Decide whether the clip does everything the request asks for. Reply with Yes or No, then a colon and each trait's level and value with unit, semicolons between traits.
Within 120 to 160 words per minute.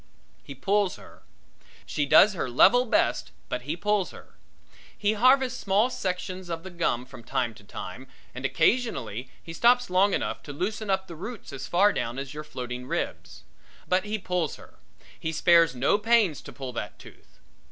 No: average, 180 wpm